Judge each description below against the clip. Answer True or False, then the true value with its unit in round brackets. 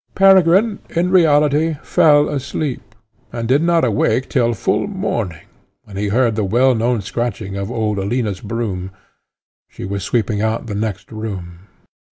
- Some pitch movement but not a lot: False (6.2 semitones)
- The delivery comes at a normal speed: True (150 wpm)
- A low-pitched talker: True (115 Hz)